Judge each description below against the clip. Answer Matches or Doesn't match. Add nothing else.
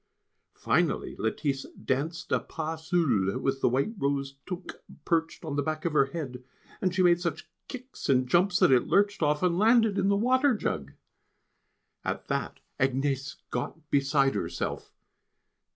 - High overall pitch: Doesn't match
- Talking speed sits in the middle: Matches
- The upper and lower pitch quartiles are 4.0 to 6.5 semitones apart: Matches